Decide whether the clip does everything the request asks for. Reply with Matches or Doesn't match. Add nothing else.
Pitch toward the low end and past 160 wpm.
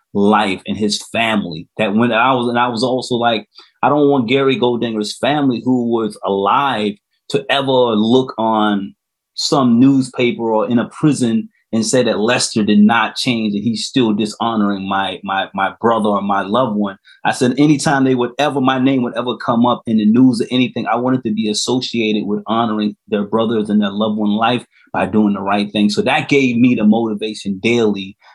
Matches